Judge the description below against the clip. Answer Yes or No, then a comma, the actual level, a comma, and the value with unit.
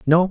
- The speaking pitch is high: No, medium, 170 Hz